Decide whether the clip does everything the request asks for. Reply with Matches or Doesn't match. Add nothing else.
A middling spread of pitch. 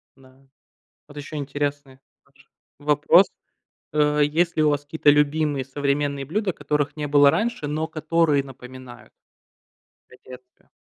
Doesn't match